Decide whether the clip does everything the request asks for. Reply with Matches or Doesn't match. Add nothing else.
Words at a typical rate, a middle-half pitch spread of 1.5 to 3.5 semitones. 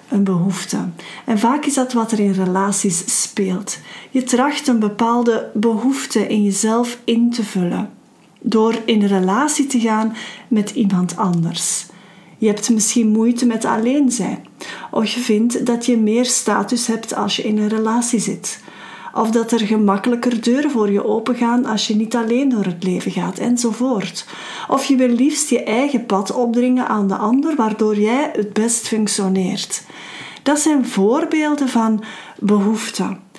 Matches